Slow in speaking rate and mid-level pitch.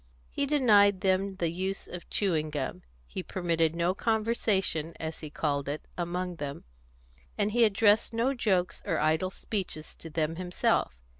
No: average, 155 wpm; medium, 180 Hz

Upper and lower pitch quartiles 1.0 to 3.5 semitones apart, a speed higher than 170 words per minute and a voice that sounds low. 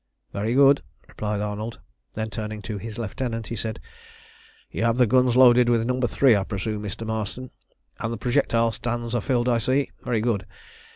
Yes: narrow, 2.4 semitones; average, 180 wpm; low, 115 Hz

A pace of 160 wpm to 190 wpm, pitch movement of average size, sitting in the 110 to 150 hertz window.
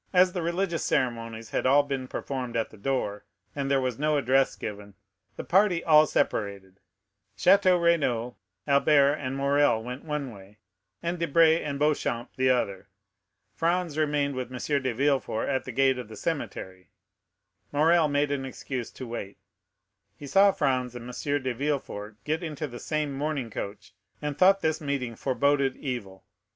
Yes: average, 165 wpm; average, 3.9 semitones; medium, 140 Hz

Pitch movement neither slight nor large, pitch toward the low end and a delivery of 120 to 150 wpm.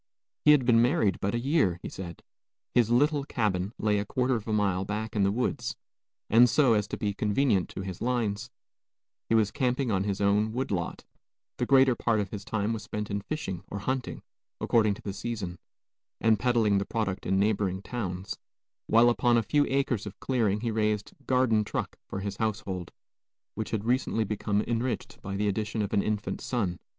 No: average, 3.2 semitones; low, 110 Hz; average, 195 wpm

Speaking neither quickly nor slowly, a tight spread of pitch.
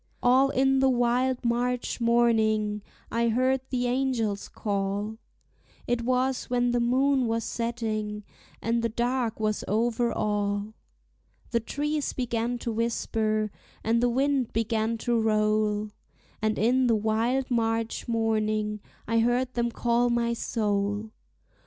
No: slow, 130 wpm; narrow, 2.2 semitones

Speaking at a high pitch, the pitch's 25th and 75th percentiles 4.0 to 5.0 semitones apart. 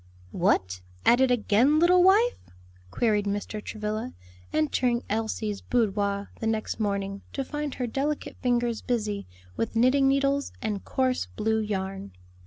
Yes: high, 225 Hz; average, 4.3 semitones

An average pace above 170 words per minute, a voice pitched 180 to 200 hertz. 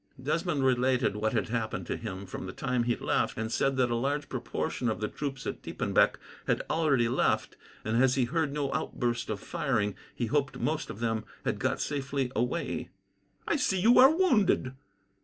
No: average, 190 wpm; low, 130 Hz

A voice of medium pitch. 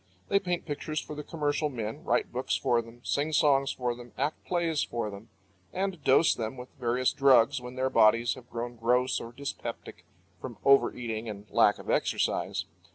No: low, 130 Hz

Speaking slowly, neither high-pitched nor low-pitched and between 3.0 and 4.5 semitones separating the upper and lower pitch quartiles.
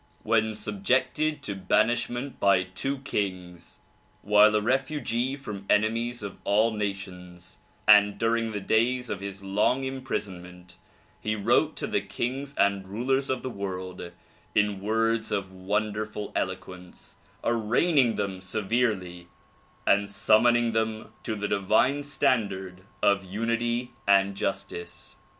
No: slow, 125 wpm; low, 105 Hz; average, 3.5 semitones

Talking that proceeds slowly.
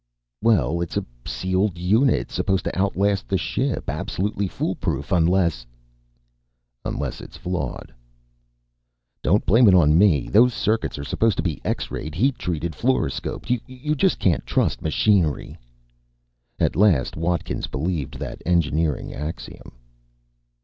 Yes: slow, 130 wpm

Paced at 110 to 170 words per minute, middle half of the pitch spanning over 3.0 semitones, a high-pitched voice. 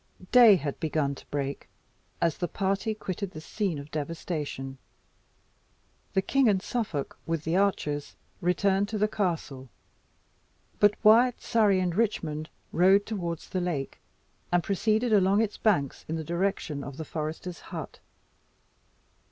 No: average, 140 wpm; average, 4.8 semitones; medium, 180 Hz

